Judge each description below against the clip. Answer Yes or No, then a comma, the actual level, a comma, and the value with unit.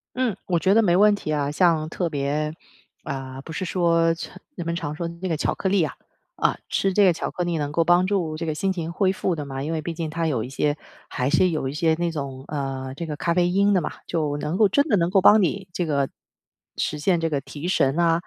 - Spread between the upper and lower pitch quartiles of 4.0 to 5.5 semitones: No, average, 3.4 semitones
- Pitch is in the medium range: Yes, medium, 165 Hz